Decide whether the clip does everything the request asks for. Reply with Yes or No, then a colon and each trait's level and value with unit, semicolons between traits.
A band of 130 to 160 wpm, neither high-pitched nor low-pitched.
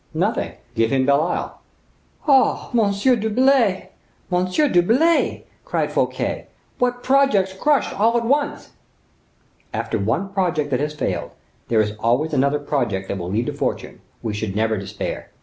Yes: average, 150 wpm; medium, 180 Hz